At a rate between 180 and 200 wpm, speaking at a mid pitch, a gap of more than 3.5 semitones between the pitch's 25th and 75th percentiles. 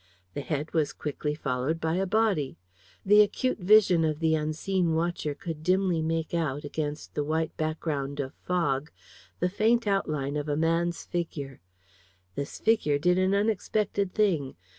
No: average, 155 wpm; medium, 160 Hz; average, 4.0 semitones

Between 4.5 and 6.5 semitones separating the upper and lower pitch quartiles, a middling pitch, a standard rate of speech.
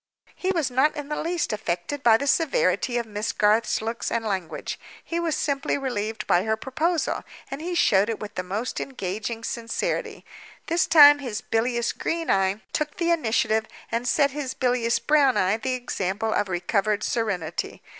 No: wide, 5.4 semitones; high, 235 Hz; average, 170 wpm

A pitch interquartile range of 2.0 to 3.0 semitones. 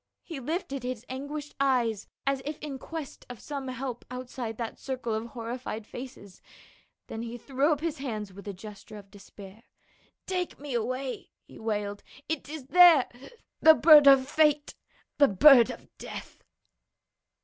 No: average, 4.4 semitones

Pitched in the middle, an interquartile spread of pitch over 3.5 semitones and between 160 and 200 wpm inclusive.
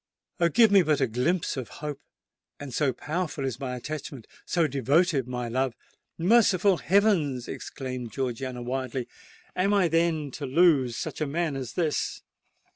No: medium, 145 Hz; average, 5.2 semitones; average, 145 wpm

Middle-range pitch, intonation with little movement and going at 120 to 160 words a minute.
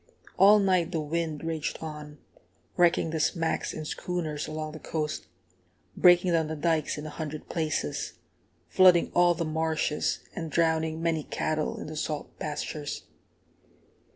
Yes: medium, 160 Hz; narrow, 1.7 semitones; average, 145 wpm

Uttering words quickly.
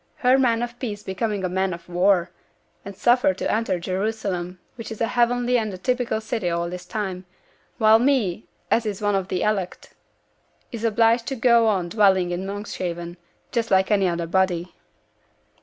No: average, 175 wpm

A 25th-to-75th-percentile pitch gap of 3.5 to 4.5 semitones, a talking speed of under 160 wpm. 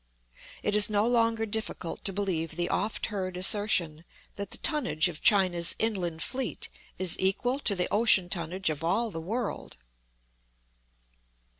Yes: average, 4.2 semitones; average, 145 wpm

